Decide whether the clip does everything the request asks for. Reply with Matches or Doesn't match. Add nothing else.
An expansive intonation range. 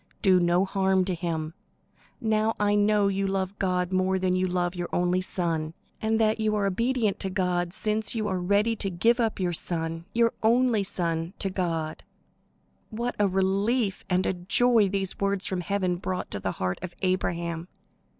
Doesn't match